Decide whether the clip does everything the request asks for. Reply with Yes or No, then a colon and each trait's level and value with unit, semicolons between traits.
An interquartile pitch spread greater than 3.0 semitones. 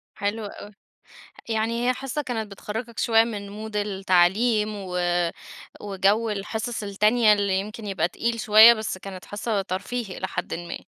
No: narrow, 2.5 semitones